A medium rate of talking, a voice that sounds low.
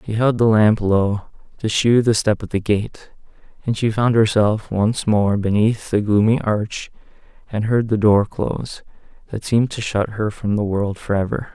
Yes: average, 190 wpm; low, 110 Hz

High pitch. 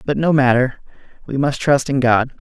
No: low, 135 Hz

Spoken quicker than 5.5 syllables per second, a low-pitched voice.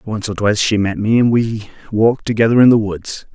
Yes: 5.9 syllables/s; low, 110 Hz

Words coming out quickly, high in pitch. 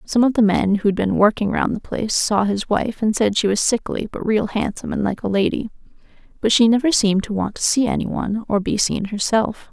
Yes: fast, 235 wpm; high, 215 Hz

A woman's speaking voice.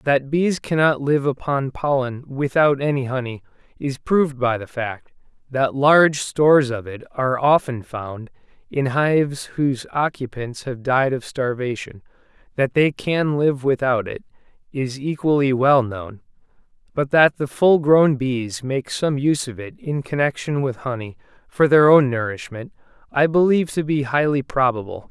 No: male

